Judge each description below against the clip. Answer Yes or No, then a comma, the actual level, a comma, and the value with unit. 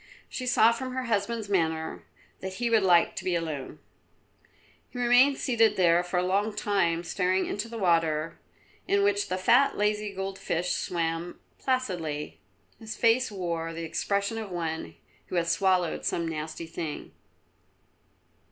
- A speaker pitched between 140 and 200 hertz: Yes, high, 190 Hz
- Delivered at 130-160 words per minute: Yes, average, 150 wpm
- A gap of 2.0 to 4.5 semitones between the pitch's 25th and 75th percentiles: No, average, 5.2 semitones